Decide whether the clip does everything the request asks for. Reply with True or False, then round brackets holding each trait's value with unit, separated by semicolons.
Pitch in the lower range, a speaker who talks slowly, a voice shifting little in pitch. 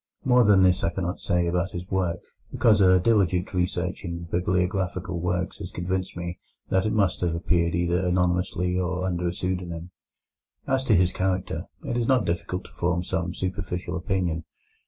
False (90 Hz; 175 wpm; 1.3 semitones)